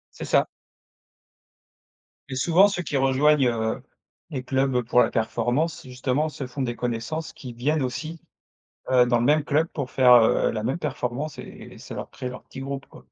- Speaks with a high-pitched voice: No, low, 130 Hz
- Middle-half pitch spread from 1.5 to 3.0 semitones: No, average, 3.5 semitones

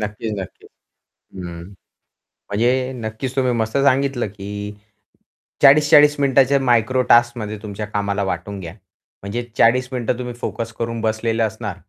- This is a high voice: No, low, 115 Hz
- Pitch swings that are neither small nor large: Yes, average, 3.7 semitones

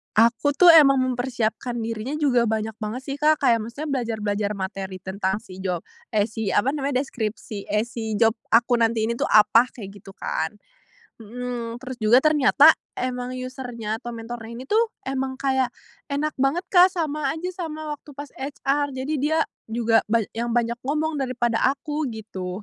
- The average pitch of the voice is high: Yes, high, 245 Hz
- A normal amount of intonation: Yes, average, 3.9 semitones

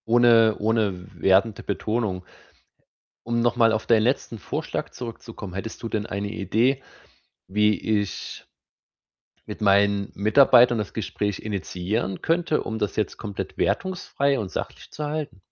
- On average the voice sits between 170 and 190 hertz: No, low, 110 Hz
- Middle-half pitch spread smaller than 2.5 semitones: No, average, 2.9 semitones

